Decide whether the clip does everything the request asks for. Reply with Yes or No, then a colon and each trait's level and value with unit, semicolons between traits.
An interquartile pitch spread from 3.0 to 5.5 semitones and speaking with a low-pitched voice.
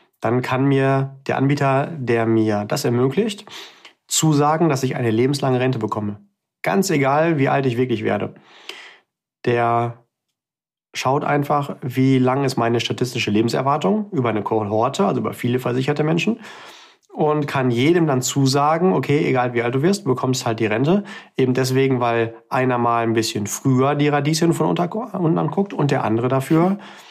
Yes: average, 4.0 semitones; low, 130 Hz